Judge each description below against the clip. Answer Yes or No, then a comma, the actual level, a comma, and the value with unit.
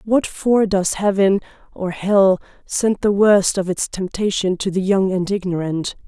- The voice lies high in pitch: Yes, high, 195 Hz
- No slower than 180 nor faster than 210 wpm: No, average, 150 wpm